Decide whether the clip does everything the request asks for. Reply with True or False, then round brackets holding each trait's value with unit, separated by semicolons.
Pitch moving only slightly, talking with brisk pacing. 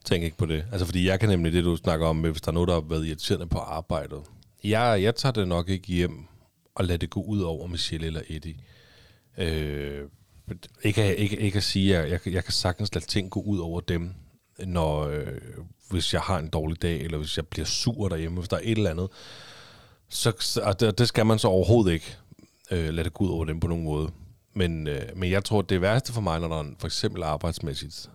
False (4.1 semitones; 230 wpm)